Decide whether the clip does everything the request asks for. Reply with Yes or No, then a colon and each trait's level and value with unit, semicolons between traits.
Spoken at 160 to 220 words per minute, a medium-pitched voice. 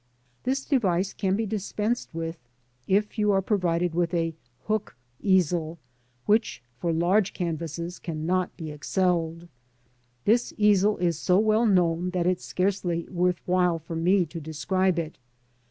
No: average, 145 wpm; medium, 180 Hz